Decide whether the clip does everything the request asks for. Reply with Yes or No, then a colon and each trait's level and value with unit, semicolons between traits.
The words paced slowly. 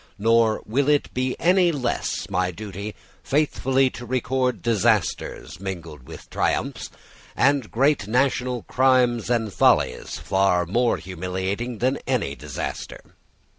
Yes: slow, 115 wpm